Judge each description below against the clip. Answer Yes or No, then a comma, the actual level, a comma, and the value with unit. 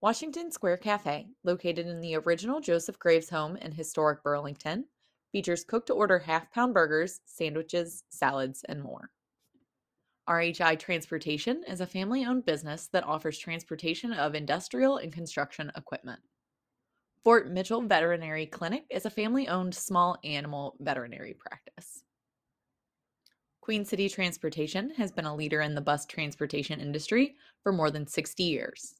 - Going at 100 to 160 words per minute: Yes, average, 140 wpm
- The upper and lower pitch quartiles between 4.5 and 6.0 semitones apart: Yes, average, 5.1 semitones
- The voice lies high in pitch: No, medium, 170 Hz